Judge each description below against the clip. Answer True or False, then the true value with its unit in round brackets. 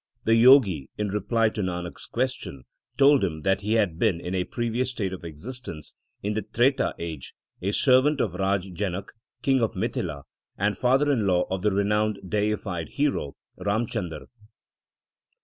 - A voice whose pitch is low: True (105 Hz)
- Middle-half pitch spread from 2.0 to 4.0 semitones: False (4.4 semitones)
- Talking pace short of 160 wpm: False (165 wpm)